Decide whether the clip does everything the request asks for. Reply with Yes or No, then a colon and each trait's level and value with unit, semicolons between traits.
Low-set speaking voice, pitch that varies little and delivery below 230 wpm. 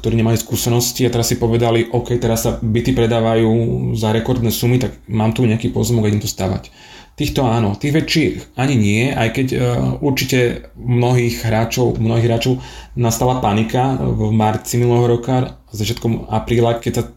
Yes: low, 115 Hz; narrow, 1.6 semitones; average, 160 wpm